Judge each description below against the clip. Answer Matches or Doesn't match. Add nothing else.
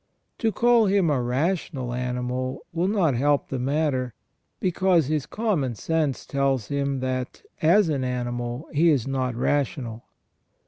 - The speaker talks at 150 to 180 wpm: Doesn't match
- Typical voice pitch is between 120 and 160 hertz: Matches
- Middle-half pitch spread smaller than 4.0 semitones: Doesn't match